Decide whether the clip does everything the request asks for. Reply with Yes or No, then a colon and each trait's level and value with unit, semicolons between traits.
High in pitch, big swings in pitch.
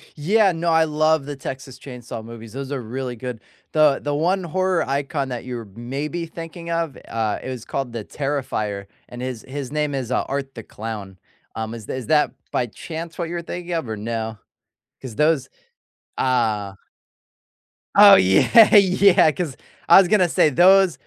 No: medium, 140 Hz; wide, 5.8 semitones